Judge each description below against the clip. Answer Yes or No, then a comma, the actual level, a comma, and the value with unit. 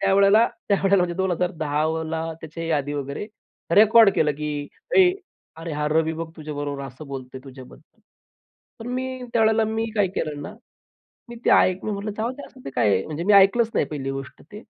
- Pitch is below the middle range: No, medium, 165 Hz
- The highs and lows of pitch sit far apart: Yes, wide, 6.0 semitones